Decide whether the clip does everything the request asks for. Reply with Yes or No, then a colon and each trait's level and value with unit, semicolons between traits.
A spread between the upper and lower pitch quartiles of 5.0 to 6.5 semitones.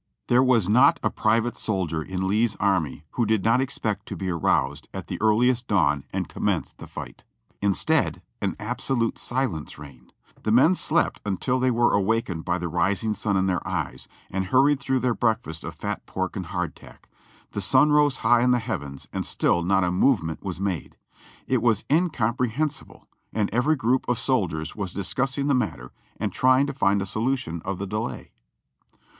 Yes: wide, 5.6 semitones